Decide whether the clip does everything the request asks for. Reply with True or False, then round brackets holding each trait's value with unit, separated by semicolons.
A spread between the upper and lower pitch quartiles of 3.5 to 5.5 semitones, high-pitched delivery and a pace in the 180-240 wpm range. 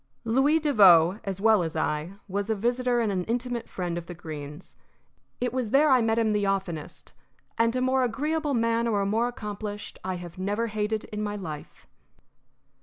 True (4.3 semitones; 215 Hz; 185 wpm)